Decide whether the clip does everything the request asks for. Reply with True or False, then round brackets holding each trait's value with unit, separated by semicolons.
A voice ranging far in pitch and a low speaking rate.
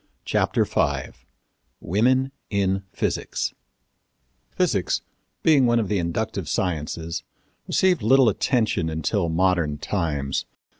True (6.3 semitones; 100 wpm)